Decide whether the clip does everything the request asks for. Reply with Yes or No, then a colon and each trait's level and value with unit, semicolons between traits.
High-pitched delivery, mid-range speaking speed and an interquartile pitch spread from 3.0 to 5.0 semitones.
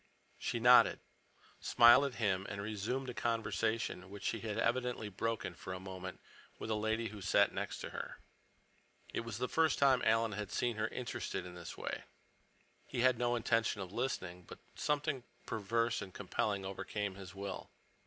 No: low, 110 Hz; average, 175 wpm; average, 3.4 semitones